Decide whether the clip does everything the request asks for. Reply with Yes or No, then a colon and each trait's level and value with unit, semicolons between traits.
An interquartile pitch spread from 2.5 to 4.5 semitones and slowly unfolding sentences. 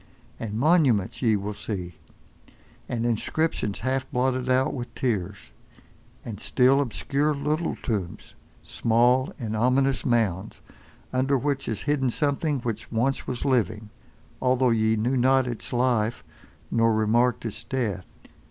Yes: average, 3.2 semitones; slow, 130 wpm